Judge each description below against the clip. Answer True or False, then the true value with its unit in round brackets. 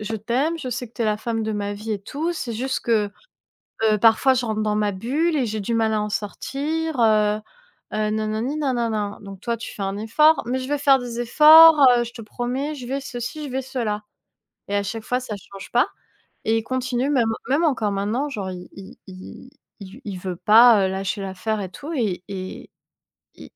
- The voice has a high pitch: True (225 Hz)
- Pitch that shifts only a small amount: False (3.8 semitones)